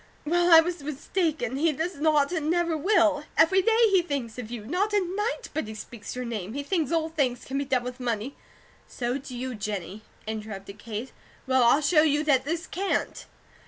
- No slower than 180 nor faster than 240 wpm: Yes, fast, 205 wpm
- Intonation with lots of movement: Yes, wide, 5.7 semitones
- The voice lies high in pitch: Yes, very high, 285 Hz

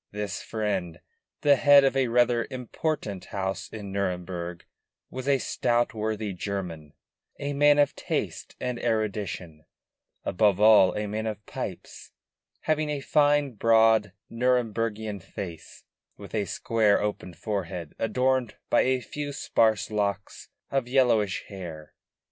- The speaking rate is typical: No, slow, 130 wpm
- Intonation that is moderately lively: Yes, average, 4.3 semitones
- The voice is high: No, low, 110 Hz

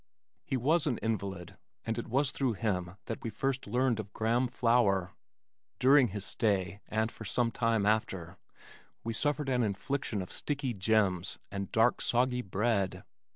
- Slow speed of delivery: No, average, 155 wpm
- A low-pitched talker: Yes, low, 115 Hz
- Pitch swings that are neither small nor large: Yes, average, 3.8 semitones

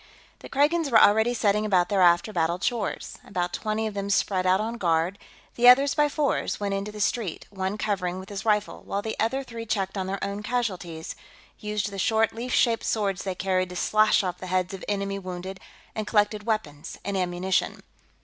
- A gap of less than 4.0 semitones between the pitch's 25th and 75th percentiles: Yes, average, 3.0 semitones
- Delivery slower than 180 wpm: No, average, 200 wpm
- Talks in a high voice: Yes, high, 200 Hz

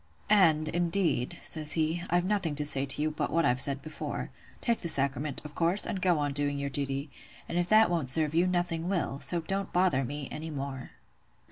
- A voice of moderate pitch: Yes, medium, 155 Hz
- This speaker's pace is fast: Yes, fast, 210 wpm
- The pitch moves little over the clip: No, average, 3.8 semitones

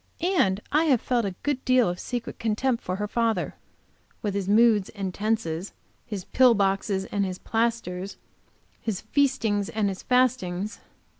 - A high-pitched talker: Yes, high, 215 Hz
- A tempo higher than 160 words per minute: No, average, 155 wpm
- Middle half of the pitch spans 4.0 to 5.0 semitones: No, average, 3.5 semitones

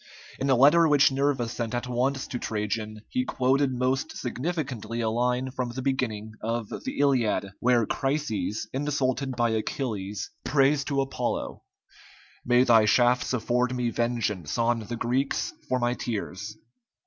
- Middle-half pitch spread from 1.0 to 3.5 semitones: Yes, average, 2.7 semitones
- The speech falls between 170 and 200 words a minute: No, average, 150 wpm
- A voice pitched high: No, low, 125 Hz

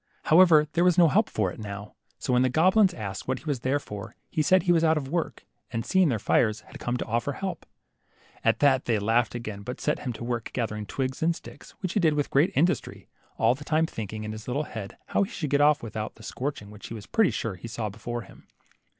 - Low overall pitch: Yes, low, 130 Hz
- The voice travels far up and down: Yes, wide, 6.4 semitones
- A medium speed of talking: No, fast, 250 wpm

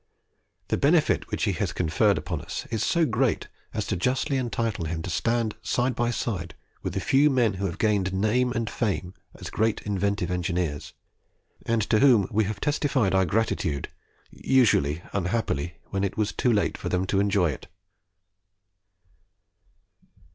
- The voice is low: Yes, low, 105 Hz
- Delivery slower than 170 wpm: Yes, average, 160 wpm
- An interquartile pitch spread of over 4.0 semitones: Yes, average, 4.6 semitones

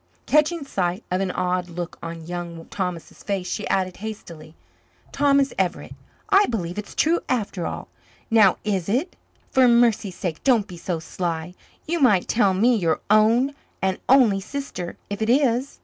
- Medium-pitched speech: No, high, 200 Hz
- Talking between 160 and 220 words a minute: Yes, average, 165 wpm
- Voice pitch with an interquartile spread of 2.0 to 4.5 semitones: No, wide, 5.6 semitones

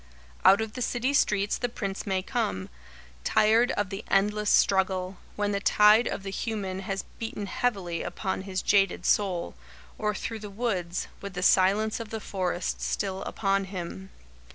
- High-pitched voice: Yes, high, 200 Hz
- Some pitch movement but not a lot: No, narrow, 2.2 semitones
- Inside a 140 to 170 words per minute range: Yes, average, 165 wpm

